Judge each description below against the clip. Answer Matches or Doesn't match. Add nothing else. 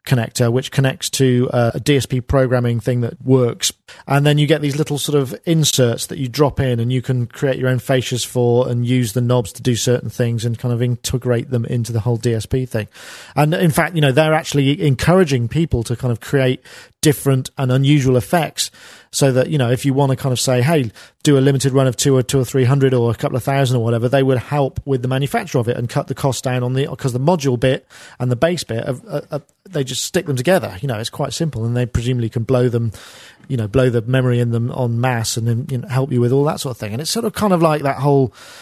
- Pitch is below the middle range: Matches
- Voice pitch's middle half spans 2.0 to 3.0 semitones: Matches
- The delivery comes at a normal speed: Doesn't match